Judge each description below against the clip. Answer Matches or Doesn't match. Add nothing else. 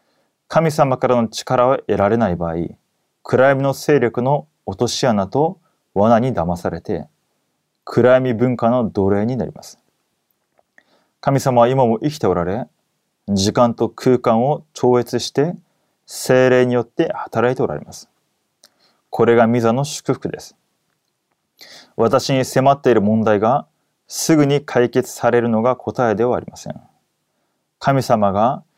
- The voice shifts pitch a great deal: Doesn't match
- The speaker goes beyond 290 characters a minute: Doesn't match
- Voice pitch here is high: Doesn't match